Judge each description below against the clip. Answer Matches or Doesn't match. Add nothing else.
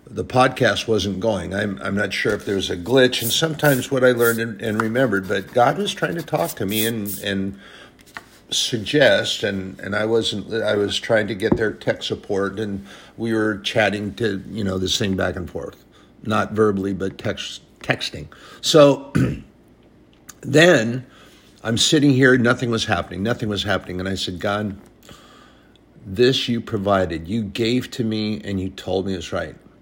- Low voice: Matches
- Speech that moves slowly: Doesn't match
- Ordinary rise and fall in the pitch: Matches